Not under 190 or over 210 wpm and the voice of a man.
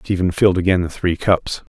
Yes: fast, 205 wpm; male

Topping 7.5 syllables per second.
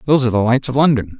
Yes: 7.8 syllables/s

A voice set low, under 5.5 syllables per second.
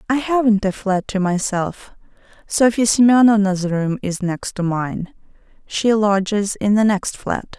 No: high, 205 Hz; 4.1 syllables/s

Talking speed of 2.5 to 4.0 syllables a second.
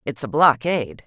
No: 5.3 syllables/s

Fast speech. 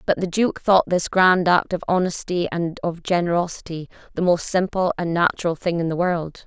No: average, 195 wpm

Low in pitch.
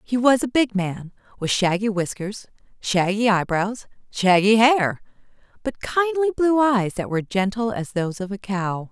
No: high, 215 Hz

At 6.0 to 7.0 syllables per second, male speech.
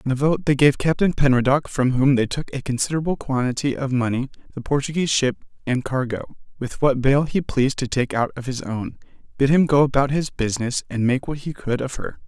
No: 4.9 syllables/s; male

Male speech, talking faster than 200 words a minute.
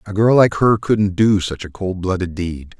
Yes: male; fast, 235 wpm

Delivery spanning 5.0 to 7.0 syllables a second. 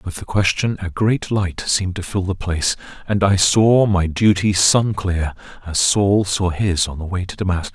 No: 4.8 syllables/s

